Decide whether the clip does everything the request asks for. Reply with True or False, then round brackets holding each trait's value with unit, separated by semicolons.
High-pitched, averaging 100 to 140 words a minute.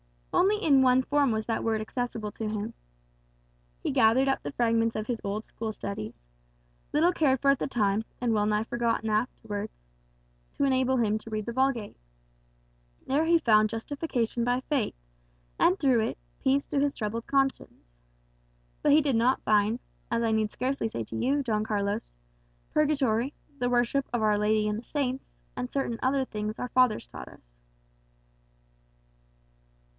False (235 Hz; 165 wpm)